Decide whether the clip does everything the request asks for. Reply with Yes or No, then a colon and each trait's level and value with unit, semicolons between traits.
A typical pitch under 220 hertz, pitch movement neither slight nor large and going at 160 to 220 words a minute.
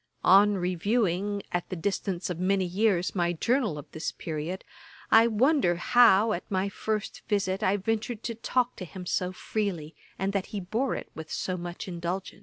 Yes: high, 190 Hz; average, 3.4 semitones; average, 180 wpm